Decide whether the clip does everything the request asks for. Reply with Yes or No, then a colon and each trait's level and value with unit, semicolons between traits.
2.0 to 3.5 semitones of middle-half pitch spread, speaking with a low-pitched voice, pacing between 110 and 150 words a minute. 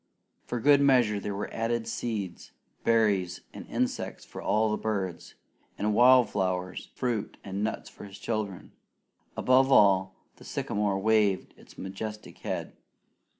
Yes: average, 2.8 semitones; low, 105 Hz; slow, 135 wpm